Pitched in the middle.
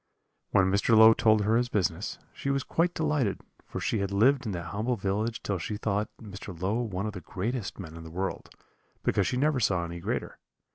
No: low, 105 Hz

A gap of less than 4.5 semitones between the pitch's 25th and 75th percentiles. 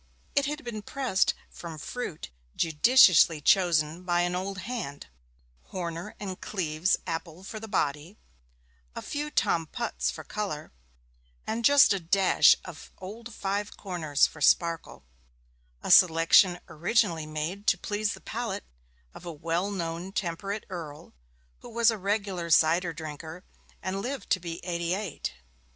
Yes: average, 4.0 semitones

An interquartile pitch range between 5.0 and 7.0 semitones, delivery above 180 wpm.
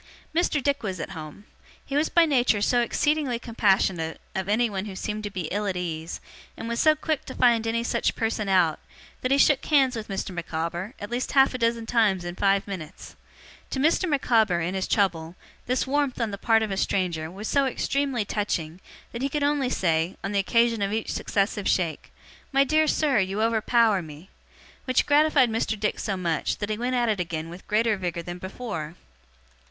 Yes: average, 5.3 semitones; average, 200 wpm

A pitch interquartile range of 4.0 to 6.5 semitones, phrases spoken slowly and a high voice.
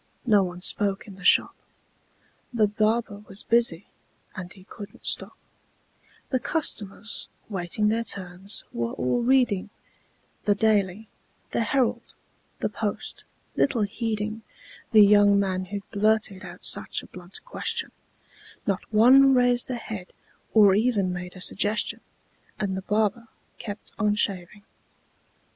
No: average, 2.8 semitones; slow, 130 wpm; high, 210 Hz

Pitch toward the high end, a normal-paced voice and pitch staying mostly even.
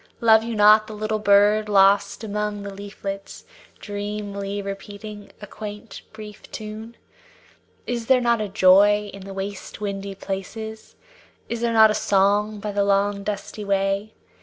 Yes: high, 205 Hz; average, 150 wpm; narrow, 1.4 semitones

